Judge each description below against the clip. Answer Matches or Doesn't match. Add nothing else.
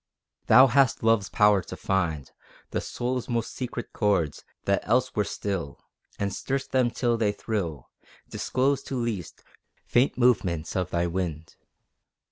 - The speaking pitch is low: Matches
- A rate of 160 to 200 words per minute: Doesn't match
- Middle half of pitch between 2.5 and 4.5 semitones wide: Doesn't match